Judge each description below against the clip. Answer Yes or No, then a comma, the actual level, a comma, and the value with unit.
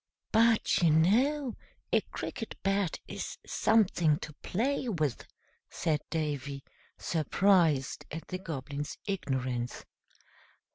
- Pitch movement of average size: No, wide, 5.7 semitones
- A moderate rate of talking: No, slow, 100 wpm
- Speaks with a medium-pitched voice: Yes, medium, 165 Hz